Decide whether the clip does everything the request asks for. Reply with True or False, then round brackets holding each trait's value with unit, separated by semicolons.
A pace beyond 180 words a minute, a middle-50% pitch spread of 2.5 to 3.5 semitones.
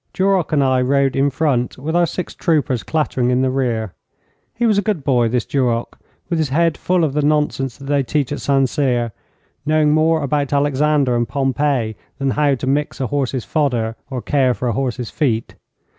True (200 wpm; 3.0 semitones)